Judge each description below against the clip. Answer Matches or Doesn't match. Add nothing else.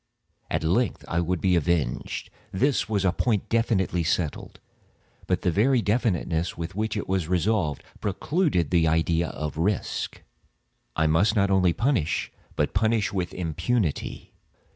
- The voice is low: Matches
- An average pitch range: Matches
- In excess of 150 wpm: Doesn't match